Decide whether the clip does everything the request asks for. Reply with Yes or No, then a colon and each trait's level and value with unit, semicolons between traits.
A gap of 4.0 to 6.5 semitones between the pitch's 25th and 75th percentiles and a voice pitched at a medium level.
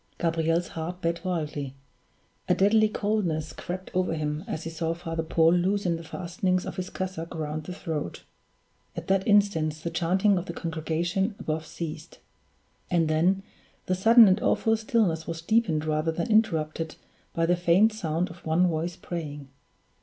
No: average, 2.8 semitones; medium, 170 Hz